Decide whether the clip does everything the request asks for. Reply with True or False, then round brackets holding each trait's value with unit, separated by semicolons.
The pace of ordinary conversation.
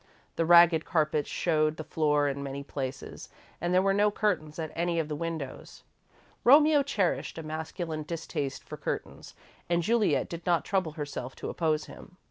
True (170 wpm)